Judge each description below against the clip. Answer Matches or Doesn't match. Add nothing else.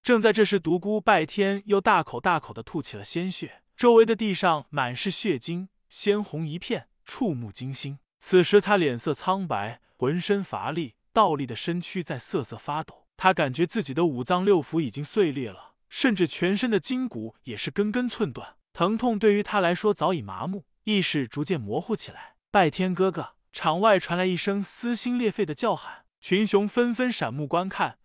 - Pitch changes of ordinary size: Matches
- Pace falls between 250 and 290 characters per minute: Matches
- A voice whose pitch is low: Doesn't match